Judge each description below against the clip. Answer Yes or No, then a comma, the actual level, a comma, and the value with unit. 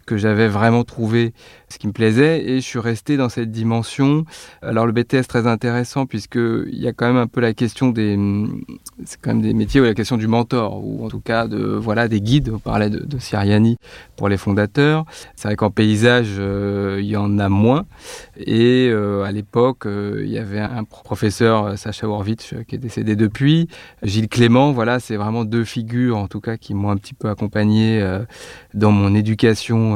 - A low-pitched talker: Yes, low, 115 Hz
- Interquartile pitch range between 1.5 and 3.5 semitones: Yes, narrow, 2.4 semitones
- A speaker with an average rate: Yes, average, 205 wpm